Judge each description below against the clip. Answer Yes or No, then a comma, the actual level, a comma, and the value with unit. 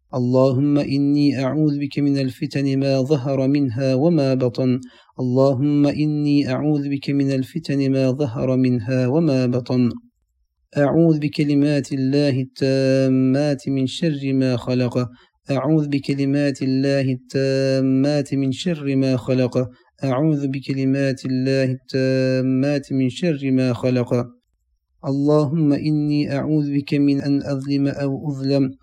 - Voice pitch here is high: No, low, 135 Hz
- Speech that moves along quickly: No, average, 115 wpm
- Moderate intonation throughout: No, narrow, 1.8 semitones